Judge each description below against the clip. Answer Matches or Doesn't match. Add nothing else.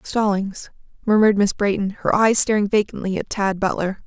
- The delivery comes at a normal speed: Matches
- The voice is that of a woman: Matches